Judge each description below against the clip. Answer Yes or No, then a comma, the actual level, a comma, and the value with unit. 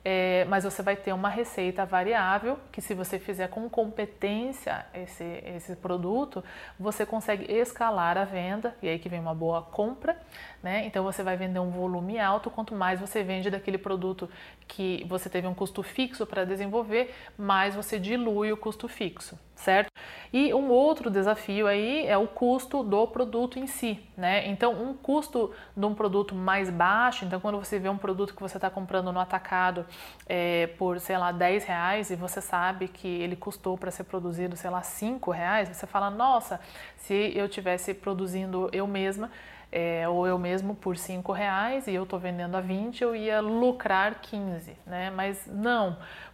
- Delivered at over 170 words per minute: Yes, average, 180 wpm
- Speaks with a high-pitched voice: Yes, high, 195 Hz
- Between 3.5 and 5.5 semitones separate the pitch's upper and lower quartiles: No, average, 2.9 semitones